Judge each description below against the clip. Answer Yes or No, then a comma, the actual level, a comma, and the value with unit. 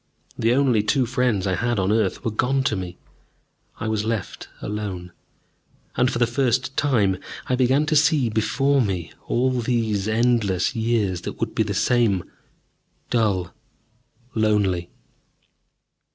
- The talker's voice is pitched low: Yes, low, 115 Hz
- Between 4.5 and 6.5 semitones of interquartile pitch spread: No, average, 4.0 semitones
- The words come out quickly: No, average, 140 wpm